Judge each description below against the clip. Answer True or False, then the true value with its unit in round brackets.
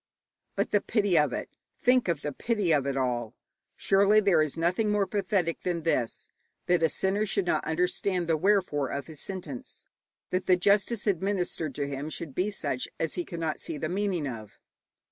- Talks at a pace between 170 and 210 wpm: True (185 wpm)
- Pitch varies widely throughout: False (4.9 semitones)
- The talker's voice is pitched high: False (175 Hz)